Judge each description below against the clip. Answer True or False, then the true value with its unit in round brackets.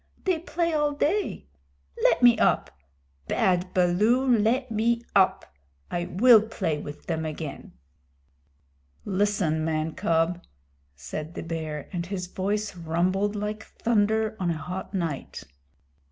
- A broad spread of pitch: False (5.0 semitones)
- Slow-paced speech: True (130 wpm)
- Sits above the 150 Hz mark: True (190 Hz)